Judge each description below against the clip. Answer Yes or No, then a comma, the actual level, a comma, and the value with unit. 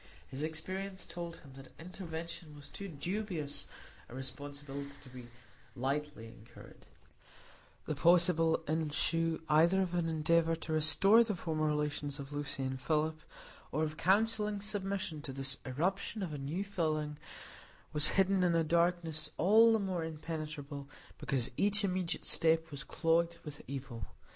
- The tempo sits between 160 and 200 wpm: No, average, 145 wpm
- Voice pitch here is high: No, medium, 160 Hz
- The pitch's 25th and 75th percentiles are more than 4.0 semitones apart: No, average, 3.6 semitones